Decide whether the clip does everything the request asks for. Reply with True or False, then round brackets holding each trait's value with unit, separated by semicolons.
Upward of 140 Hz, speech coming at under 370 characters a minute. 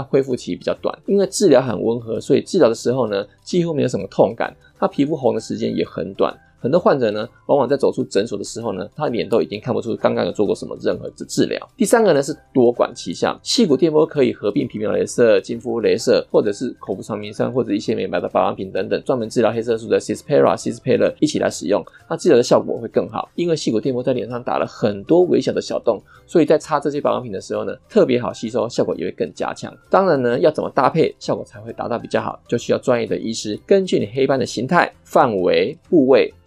False (185 Hz; 390 characters per minute)